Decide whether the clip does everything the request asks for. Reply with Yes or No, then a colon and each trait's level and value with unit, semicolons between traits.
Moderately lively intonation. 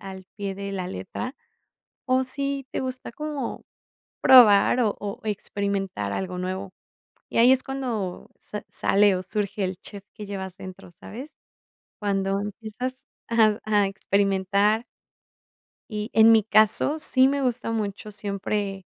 Yes: average, 3.5 semitones